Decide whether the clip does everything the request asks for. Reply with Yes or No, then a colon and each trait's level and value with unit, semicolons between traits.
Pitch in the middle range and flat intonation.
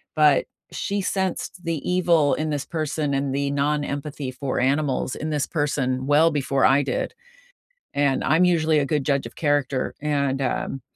Yes: medium, 145 Hz; narrow, 2.2 semitones